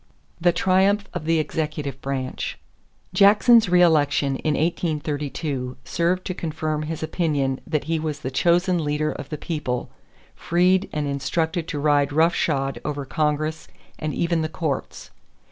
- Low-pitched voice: No, medium, 155 Hz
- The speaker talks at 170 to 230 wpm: No, average, 145 wpm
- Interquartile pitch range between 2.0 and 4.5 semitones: Yes, average, 2.9 semitones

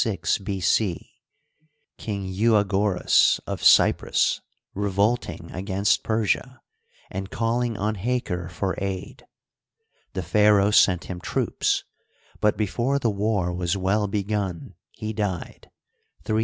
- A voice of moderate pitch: No, low, 100 Hz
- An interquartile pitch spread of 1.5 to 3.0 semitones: Yes, narrow, 2.5 semitones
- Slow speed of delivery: Yes, slow, 105 wpm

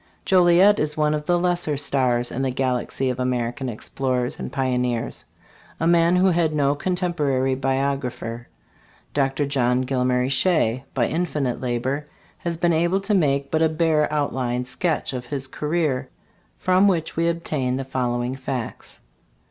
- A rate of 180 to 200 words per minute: No, average, 155 wpm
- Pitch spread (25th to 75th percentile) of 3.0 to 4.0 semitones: No, average, 4.5 semitones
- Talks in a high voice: No, medium, 140 Hz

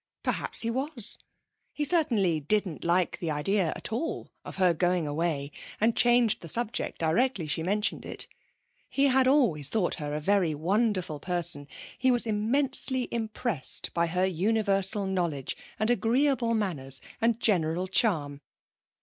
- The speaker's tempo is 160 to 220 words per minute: No, average, 145 wpm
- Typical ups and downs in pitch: No, wide, 6.1 semitones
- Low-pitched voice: No, high, 195 Hz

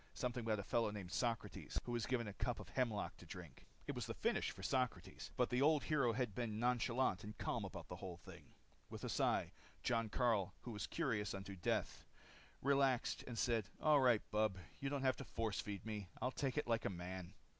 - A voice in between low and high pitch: No, low, 115 Hz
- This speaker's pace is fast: Yes, fast, 215 wpm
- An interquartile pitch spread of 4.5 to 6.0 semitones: No, average, 3.7 semitones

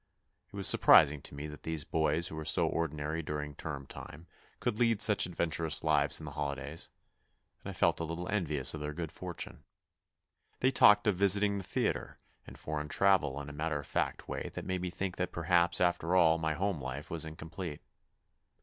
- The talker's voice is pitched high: No, very low, 80 Hz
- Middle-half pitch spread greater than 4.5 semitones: No, average, 3.2 semitones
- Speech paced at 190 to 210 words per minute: Yes, average, 195 wpm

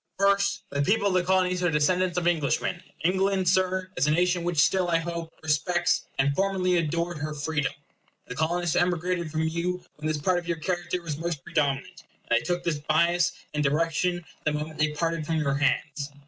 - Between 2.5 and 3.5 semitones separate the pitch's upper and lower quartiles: Yes, average, 2.9 semitones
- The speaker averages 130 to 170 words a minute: No, average, 195 wpm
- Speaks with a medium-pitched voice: Yes, medium, 170 Hz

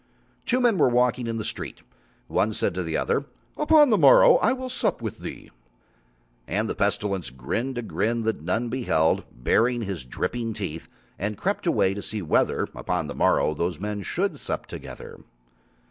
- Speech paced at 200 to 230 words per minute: No, average, 175 wpm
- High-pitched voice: No, low, 110 Hz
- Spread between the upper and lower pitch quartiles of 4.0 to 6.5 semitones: Yes, average, 5.2 semitones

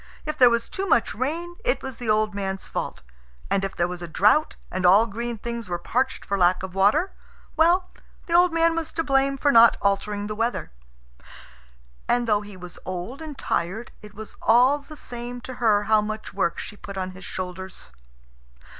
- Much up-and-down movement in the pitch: Yes, wide, 5.7 semitones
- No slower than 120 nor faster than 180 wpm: No, average, 200 wpm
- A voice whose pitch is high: Yes, high, 220 Hz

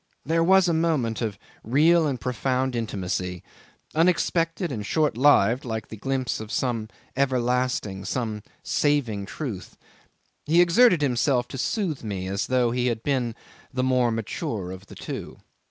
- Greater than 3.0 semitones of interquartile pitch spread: Yes, average, 5.0 semitones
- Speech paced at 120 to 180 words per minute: Yes, average, 155 wpm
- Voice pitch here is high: No, low, 125 Hz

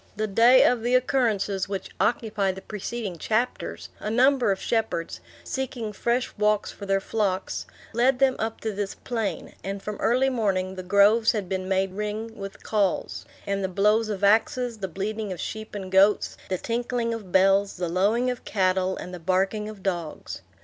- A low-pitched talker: No, high, 210 Hz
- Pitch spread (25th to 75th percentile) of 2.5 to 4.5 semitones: Yes, average, 3.1 semitones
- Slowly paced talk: No, average, 180 wpm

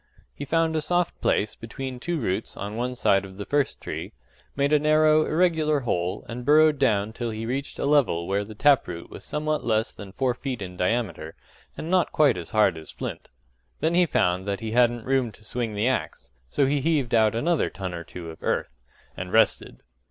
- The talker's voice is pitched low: Yes, low, 120 Hz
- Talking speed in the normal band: No, fast, 210 wpm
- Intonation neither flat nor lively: No, wide, 6.5 semitones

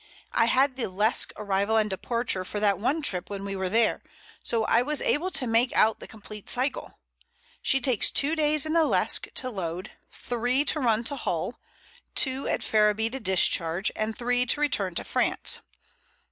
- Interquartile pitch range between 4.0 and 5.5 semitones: Yes, average, 4.5 semitones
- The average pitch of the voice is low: No, high, 225 Hz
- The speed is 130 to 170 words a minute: No, average, 185 wpm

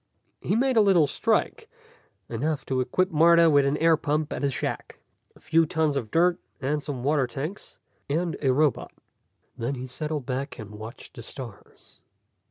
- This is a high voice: No, medium, 145 Hz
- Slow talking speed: No, average, 175 wpm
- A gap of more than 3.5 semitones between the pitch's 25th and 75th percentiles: Yes, average, 3.9 semitones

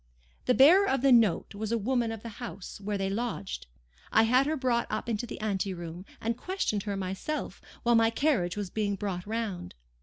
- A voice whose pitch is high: Yes, high, 220 Hz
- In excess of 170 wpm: Yes, average, 200 wpm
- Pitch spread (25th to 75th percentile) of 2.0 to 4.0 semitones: Yes, average, 3.6 semitones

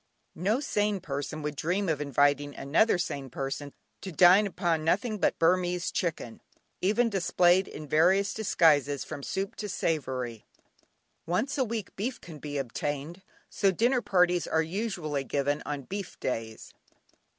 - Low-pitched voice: No, medium, 170 Hz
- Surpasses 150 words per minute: No, average, 145 wpm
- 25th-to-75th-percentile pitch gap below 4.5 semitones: No, average, 5.3 semitones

